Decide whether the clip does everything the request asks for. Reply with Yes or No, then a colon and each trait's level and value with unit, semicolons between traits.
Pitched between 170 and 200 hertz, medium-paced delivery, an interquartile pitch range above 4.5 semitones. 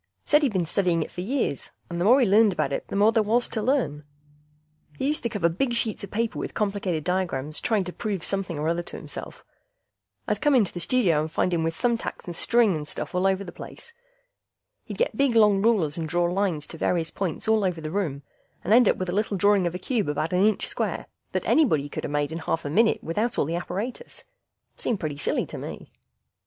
No: high, 190 Hz; fast, 240 wpm; average, 5.1 semitones